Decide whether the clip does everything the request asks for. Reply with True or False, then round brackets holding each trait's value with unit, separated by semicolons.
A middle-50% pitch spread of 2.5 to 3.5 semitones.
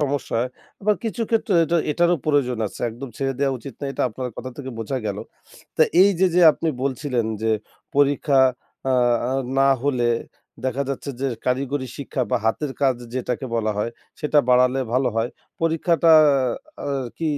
True (2.9 semitones)